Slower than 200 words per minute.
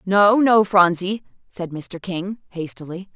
Yes: slow, 135 wpm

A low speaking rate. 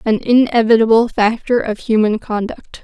Yes: slow, 125 wpm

